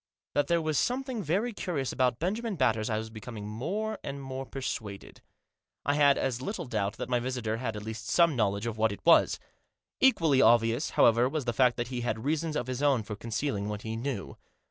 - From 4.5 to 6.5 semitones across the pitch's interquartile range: Yes, average, 5.3 semitones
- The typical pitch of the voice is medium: No, low, 125 Hz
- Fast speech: Yes, fast, 210 wpm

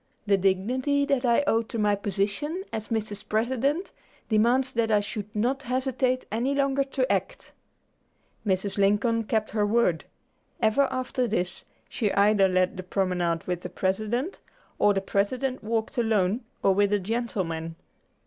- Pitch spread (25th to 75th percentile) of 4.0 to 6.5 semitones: Yes, average, 4.3 semitones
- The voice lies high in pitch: Yes, high, 220 Hz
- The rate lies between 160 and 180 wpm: No, average, 150 wpm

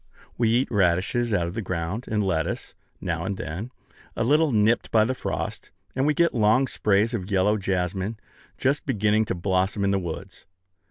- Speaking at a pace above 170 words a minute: Yes, average, 180 wpm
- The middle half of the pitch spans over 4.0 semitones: No, average, 3.7 semitones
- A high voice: No, low, 105 Hz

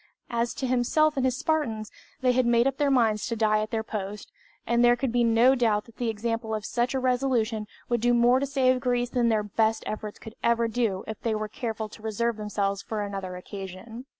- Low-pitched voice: No, high, 230 Hz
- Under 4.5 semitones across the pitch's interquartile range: Yes, narrow, 2.4 semitones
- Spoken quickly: Yes, fast, 225 wpm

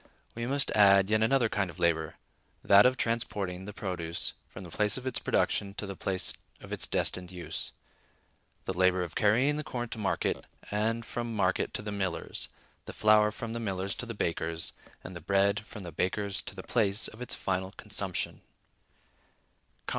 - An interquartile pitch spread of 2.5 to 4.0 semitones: Yes, average, 3.3 semitones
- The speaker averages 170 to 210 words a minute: Yes, average, 185 wpm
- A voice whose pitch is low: Yes, low, 100 Hz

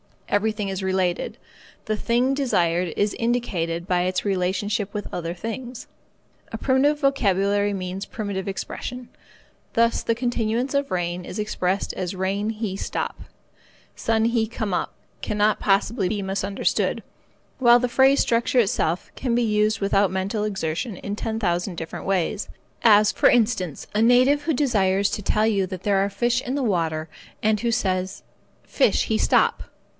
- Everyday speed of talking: Yes, average, 155 wpm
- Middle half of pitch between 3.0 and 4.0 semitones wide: Yes, average, 3.7 semitones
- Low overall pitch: No, high, 205 Hz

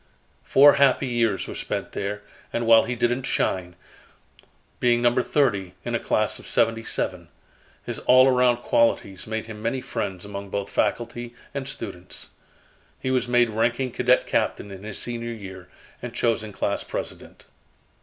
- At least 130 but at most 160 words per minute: Yes, average, 155 wpm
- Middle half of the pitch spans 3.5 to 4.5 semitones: No, average, 3.1 semitones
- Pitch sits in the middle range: No, low, 115 Hz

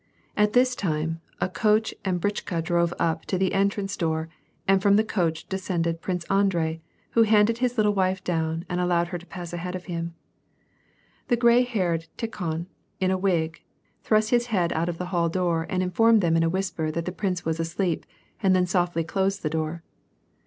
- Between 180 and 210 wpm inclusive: Yes, average, 195 wpm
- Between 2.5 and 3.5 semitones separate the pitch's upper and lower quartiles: Yes, average, 3.1 semitones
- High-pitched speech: No, medium, 180 Hz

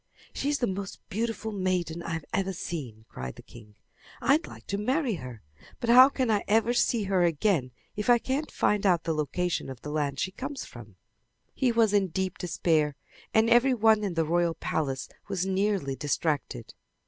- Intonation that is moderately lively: No, wide, 6.5 semitones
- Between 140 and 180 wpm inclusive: No, average, 190 wpm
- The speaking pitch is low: No, high, 190 Hz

